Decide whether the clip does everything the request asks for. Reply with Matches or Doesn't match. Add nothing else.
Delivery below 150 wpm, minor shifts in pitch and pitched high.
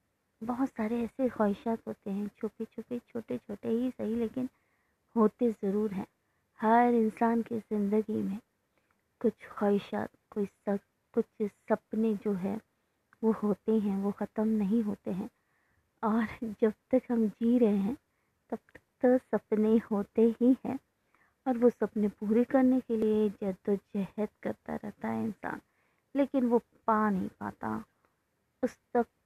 Matches